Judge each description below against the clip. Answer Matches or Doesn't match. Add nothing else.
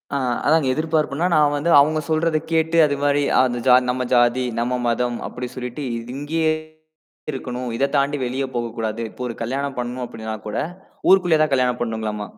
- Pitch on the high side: Doesn't match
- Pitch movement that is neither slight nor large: Matches